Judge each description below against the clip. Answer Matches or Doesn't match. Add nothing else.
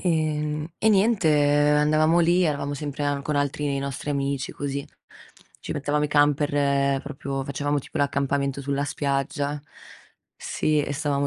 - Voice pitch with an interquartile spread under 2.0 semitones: Matches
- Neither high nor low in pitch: Matches